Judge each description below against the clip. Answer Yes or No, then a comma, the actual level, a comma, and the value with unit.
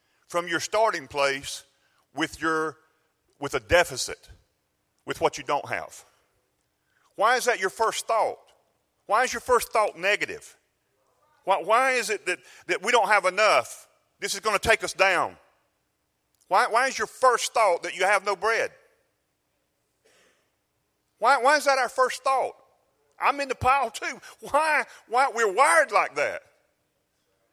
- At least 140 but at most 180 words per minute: Yes, average, 155 wpm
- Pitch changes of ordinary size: No, wide, 8.1 semitones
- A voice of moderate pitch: No, high, 245 Hz